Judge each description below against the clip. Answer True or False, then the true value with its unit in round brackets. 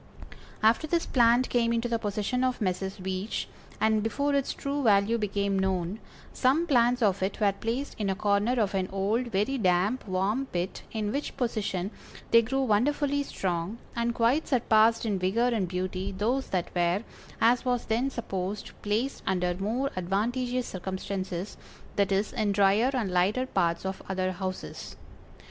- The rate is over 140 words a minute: True (160 wpm)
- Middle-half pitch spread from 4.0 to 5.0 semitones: True (4.3 semitones)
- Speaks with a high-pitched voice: True (210 Hz)